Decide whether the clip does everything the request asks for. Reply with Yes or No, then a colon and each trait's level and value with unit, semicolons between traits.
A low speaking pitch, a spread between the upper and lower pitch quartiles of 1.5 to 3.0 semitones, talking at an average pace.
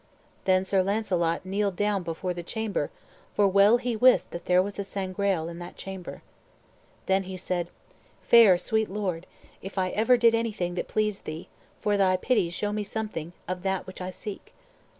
No: high, 195 Hz; narrow, 2.5 semitones; average, 180 wpm